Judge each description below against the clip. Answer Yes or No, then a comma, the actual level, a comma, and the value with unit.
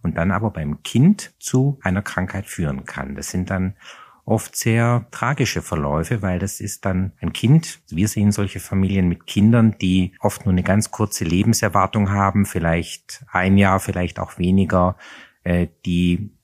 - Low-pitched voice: Yes, very low, 95 Hz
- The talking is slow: No, average, 160 wpm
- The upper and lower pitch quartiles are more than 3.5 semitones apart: No, average, 3.1 semitones